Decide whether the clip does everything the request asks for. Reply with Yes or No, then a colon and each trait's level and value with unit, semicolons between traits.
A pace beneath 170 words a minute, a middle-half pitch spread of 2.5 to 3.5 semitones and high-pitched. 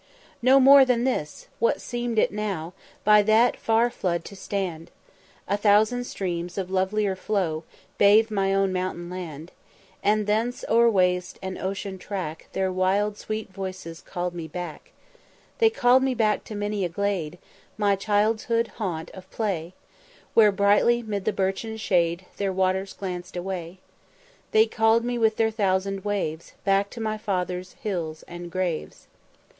Yes: average, 155 wpm; average, 3.2 semitones; high, 195 Hz